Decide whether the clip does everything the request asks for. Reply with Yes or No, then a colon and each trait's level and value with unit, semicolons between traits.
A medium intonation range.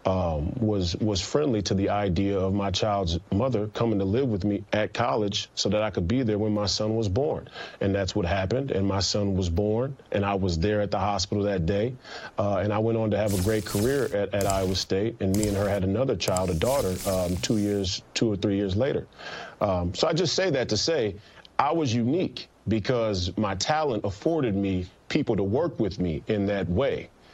No: narrow, 2.0 semitones